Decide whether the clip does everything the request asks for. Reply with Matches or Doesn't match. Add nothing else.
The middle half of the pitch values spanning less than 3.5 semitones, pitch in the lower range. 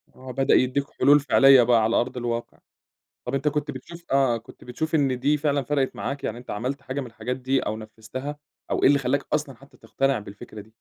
Matches